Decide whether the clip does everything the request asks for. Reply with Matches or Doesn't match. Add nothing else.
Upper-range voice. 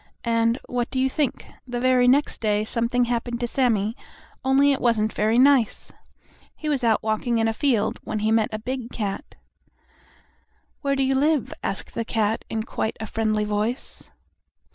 Matches